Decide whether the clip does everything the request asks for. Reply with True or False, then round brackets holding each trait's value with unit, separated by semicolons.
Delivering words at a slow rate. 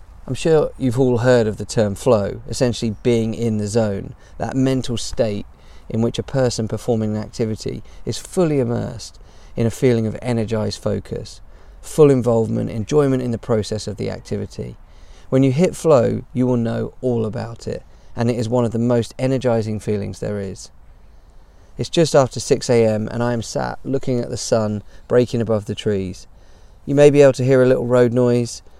False (190 wpm)